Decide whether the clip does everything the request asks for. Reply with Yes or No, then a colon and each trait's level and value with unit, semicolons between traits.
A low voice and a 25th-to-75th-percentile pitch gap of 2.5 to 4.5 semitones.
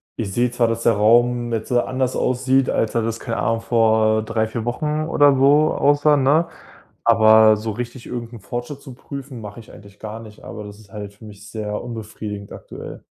Yes: low, 115 Hz; average, 2.8 semitones